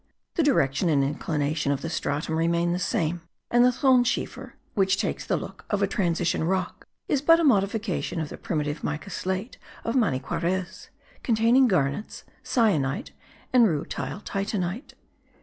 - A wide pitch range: Yes, wide, 6.4 semitones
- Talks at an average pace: Yes, average, 150 wpm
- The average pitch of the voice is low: No, medium, 185 Hz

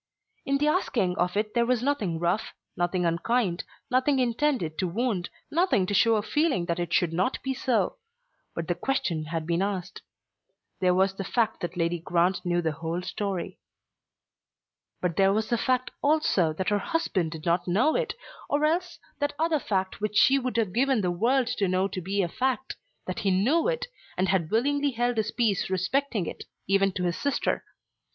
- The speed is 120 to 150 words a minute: No, average, 190 wpm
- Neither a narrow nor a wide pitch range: No, wide, 6.5 semitones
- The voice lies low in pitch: No, high, 200 Hz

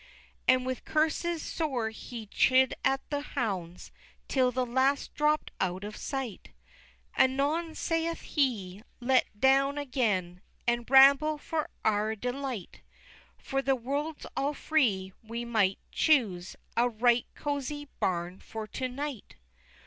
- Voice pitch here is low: No, very high, 255 Hz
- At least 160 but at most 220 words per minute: No, slow, 135 wpm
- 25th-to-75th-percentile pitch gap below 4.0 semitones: No, average, 4.5 semitones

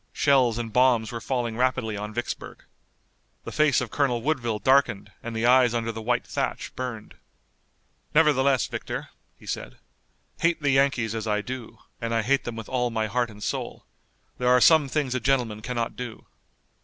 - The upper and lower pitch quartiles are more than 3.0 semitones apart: No, average, 2.7 semitones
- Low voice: Yes, low, 120 Hz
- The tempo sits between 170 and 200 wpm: Yes, average, 180 wpm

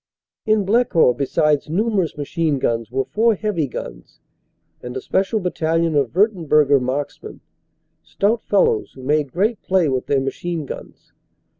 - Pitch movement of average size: No, wide, 6.5 semitones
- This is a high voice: No, medium, 160 Hz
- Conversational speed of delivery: Yes, average, 150 wpm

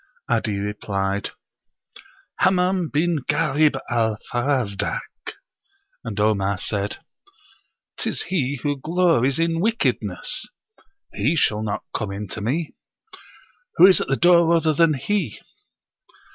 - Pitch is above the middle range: No, low, 135 Hz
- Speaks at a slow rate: Yes, slow, 115 wpm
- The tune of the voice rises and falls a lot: Yes, wide, 7.9 semitones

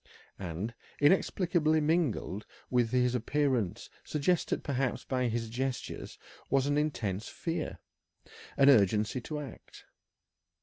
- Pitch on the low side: Yes, low, 130 Hz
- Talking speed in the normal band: No, slow, 105 wpm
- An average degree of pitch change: Yes, average, 4.6 semitones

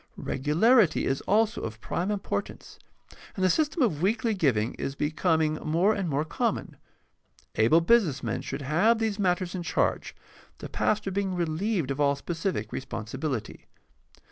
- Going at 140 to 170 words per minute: Yes, average, 150 wpm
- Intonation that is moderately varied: No, wide, 5.9 semitones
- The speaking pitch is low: No, medium, 170 Hz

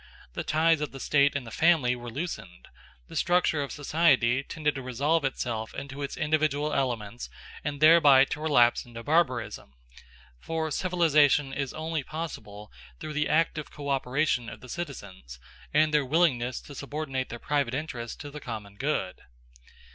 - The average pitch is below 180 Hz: Yes, medium, 140 Hz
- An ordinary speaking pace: Yes, average, 160 wpm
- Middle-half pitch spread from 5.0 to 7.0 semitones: No, average, 3.9 semitones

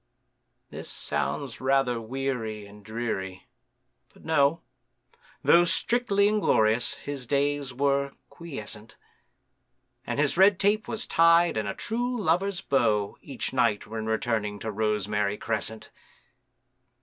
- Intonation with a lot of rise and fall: Yes, wide, 7.5 semitones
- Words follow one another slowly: Yes, slow, 115 wpm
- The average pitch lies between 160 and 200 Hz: No, low, 130 Hz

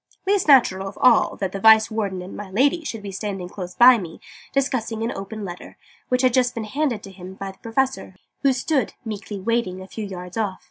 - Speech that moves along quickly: Yes, fast, 220 wpm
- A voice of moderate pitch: No, high, 215 Hz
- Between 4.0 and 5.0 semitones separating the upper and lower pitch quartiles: Yes, average, 4.6 semitones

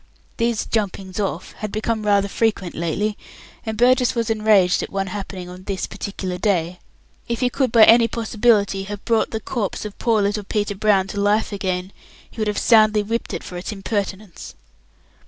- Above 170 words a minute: Yes, average, 180 wpm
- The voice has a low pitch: No, high, 205 Hz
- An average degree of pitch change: No, narrow, 2.3 semitones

